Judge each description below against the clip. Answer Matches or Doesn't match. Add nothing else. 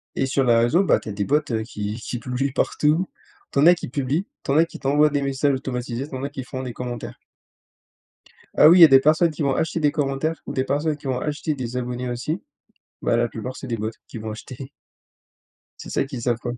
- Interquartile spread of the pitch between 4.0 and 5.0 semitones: Doesn't match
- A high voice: Doesn't match